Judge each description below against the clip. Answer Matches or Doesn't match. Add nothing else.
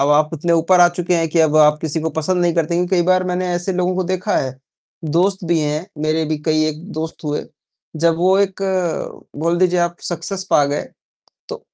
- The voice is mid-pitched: Matches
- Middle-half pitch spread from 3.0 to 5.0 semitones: Doesn't match